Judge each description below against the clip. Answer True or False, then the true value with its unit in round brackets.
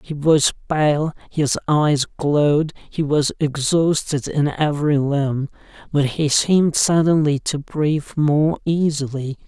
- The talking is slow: True (125 wpm)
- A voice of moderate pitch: True (150 Hz)